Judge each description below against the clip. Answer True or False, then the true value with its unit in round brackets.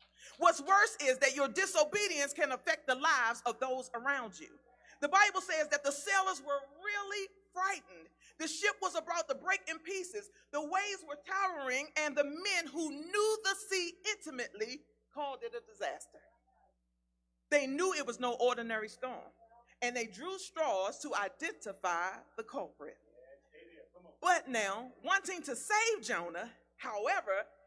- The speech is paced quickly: False (150 wpm)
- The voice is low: False (305 Hz)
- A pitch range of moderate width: False (7.5 semitones)